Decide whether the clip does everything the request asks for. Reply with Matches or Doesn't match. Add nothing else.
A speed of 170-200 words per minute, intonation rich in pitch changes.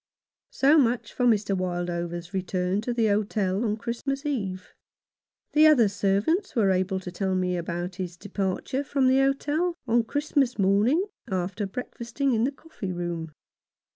Doesn't match